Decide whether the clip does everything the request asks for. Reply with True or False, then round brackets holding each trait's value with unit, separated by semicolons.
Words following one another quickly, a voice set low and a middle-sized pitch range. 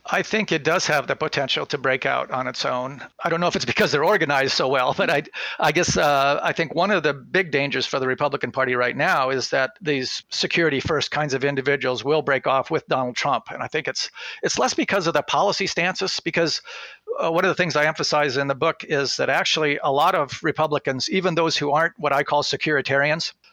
False (235 wpm; 150 Hz; 3.3 semitones)